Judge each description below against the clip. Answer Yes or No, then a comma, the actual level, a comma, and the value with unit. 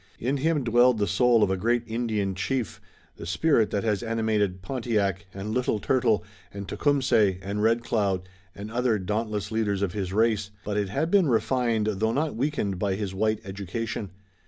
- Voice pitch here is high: No, low, 110 Hz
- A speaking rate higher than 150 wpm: Yes, average, 180 wpm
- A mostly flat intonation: No, average, 3.2 semitones